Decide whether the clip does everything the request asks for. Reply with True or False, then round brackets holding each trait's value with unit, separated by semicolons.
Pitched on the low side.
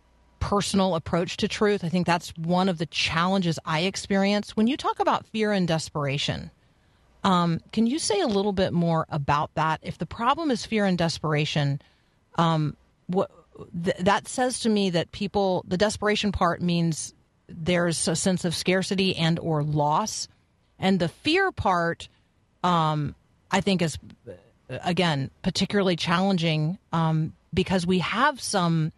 False (175 Hz)